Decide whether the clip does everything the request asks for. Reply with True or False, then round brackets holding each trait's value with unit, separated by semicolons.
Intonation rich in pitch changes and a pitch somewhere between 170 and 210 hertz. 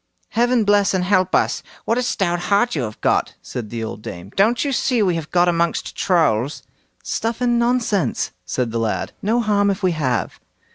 True (8.6 semitones; 185 Hz)